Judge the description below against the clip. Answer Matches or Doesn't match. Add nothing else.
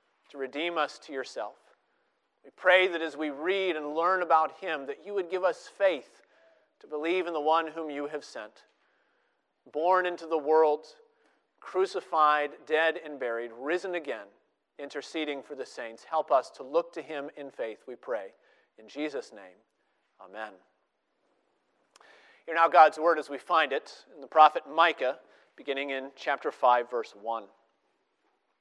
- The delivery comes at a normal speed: Matches